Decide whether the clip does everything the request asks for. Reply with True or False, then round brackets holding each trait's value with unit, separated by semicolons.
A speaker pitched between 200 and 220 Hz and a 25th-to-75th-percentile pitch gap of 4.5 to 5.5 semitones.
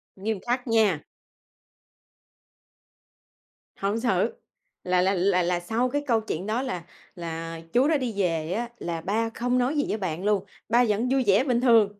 True (215 Hz; 5.2 semitones)